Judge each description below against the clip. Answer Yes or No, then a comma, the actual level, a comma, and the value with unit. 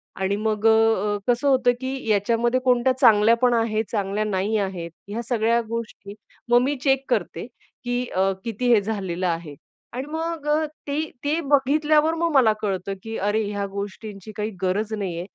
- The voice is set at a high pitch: Yes, high, 220 Hz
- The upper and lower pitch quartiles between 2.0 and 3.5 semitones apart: No, average, 3.9 semitones